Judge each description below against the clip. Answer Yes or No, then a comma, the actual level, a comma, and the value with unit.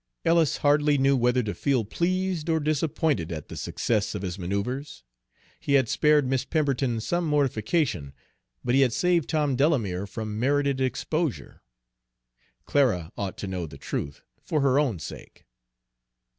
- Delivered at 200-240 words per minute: No, average, 150 wpm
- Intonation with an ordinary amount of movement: No, wide, 5.9 semitones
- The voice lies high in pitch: No, low, 135 Hz